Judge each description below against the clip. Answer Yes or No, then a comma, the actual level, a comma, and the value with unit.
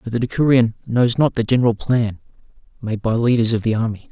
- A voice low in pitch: Yes, low, 115 Hz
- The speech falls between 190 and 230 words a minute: Yes, fast, 205 wpm